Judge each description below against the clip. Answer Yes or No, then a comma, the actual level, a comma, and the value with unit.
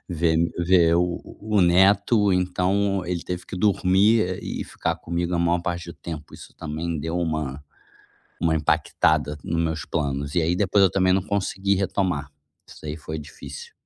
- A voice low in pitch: Yes, very low, 85 Hz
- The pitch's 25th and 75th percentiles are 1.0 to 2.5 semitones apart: No, average, 2.9 semitones